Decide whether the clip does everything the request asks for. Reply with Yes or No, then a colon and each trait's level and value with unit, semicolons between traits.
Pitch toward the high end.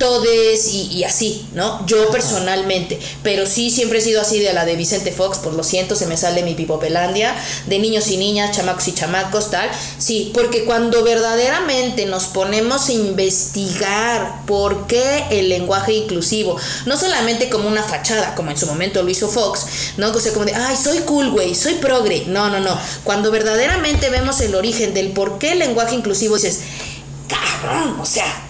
Yes: high, 210 Hz